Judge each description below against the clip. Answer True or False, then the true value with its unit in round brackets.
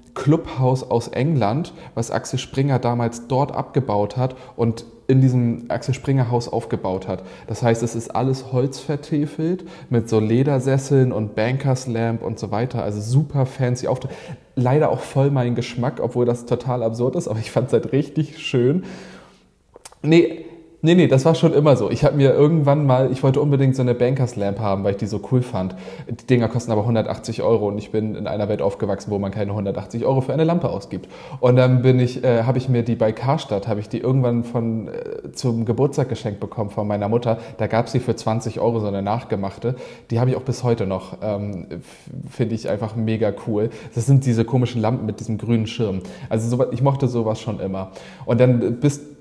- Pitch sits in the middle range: False (120 Hz)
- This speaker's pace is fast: True (205 wpm)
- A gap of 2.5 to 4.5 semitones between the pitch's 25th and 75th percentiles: True (3.2 semitones)